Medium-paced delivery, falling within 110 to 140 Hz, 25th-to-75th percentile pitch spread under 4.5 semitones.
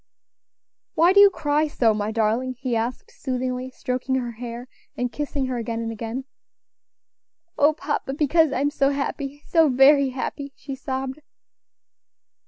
No: average, 150 wpm; very high, 265 Hz; average, 2.9 semitones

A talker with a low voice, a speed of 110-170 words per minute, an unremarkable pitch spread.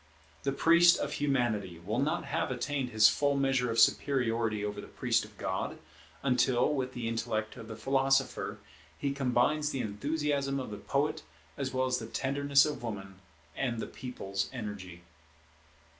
Yes: low, 125 Hz; average, 160 wpm; average, 4.1 semitones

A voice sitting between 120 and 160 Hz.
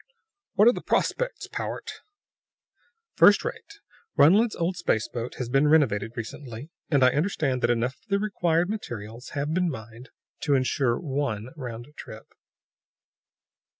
Yes: medium, 140 Hz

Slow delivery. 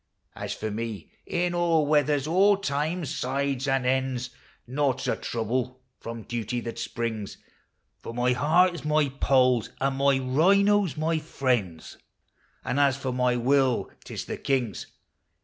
No: average, 155 wpm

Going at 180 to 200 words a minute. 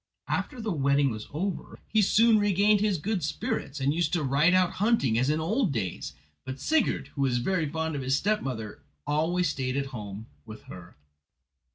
Yes: average, 185 wpm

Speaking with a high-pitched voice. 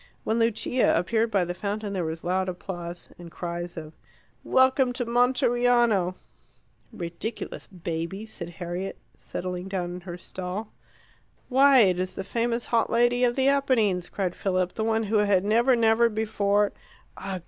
Yes: high, 200 Hz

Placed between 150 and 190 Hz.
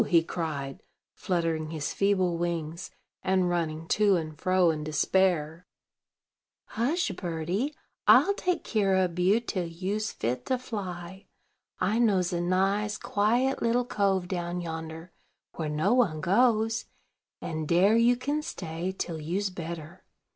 Yes: medium, 185 Hz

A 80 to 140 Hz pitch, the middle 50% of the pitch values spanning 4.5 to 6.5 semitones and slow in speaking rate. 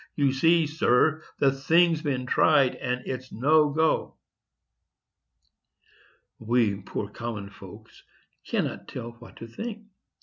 Yes: low, 135 Hz; average, 4.8 semitones; slow, 115 wpm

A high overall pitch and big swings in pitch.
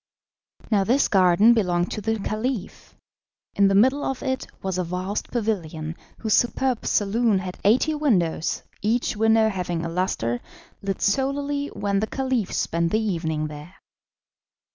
No: high, 205 Hz; average, 4.7 semitones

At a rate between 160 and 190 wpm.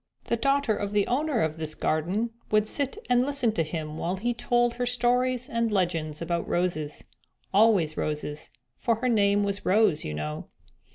Yes: average, 175 wpm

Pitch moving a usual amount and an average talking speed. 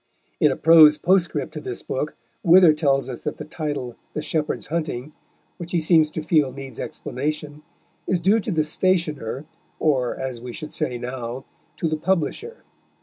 Yes: average, 3.7 semitones; average, 170 wpm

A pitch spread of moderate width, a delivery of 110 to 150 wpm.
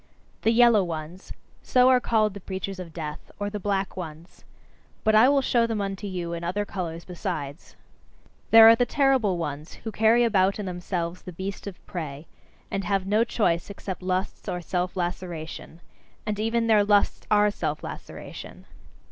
No: average, 3.7 semitones; average, 175 wpm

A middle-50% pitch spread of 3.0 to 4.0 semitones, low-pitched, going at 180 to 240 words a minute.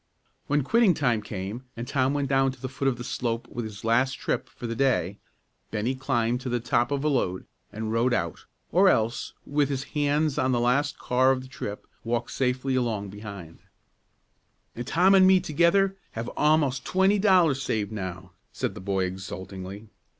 No: average, 4.6 semitones; low, 125 Hz; average, 185 wpm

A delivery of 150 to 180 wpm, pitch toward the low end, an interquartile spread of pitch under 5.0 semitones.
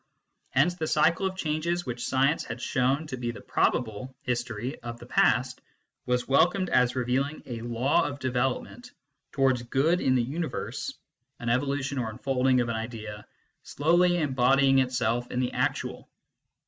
Yes: average, 160 wpm; low, 130 Hz; average, 3.2 semitones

